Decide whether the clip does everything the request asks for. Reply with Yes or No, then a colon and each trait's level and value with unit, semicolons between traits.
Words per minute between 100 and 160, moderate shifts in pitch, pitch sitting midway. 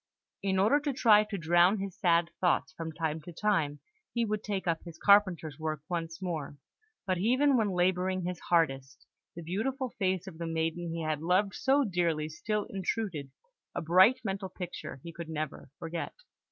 No: average, 180 wpm; average, 3.6 semitones; medium, 180 Hz